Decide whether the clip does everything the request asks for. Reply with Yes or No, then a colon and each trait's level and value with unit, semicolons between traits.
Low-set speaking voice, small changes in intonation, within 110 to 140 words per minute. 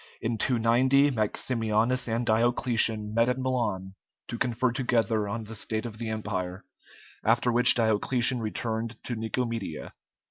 Yes: low, 115 Hz; narrow, 1.9 semitones; slow, 135 wpm